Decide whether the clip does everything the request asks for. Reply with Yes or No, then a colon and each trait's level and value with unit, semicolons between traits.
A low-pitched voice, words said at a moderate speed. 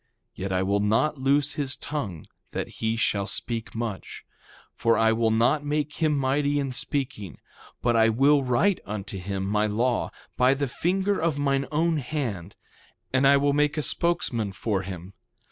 Yes: low, 125 Hz; average, 170 wpm